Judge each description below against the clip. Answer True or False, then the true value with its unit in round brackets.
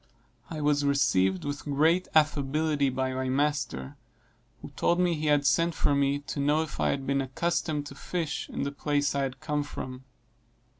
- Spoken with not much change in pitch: True (2.0 semitones)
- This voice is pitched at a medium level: True (145 Hz)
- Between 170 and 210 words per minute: True (185 wpm)